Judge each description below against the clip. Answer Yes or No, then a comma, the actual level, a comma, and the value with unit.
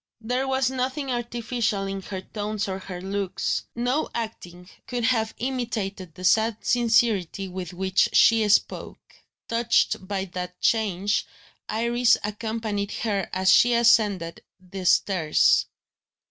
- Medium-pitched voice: No, high, 210 Hz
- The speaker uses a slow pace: Yes, slow, 125 wpm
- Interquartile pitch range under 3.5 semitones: No, average, 3.8 semitones